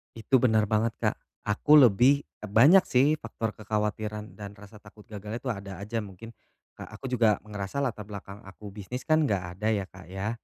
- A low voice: Yes, low, 105 Hz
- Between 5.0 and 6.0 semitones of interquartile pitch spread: No, average, 2.7 semitones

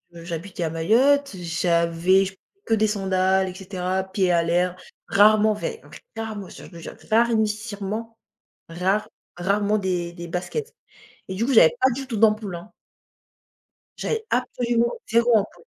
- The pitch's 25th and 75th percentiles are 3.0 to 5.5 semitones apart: Yes, average, 3.8 semitones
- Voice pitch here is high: Yes, high, 200 Hz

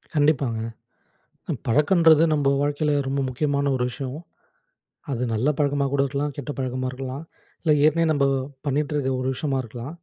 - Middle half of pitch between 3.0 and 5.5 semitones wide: No, narrow, 2.4 semitones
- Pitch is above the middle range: No, medium, 140 Hz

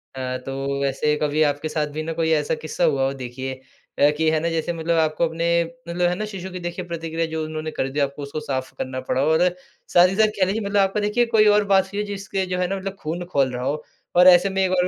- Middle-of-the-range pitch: Yes, medium, 160 Hz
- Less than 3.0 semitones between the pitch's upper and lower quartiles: No, average, 3.9 semitones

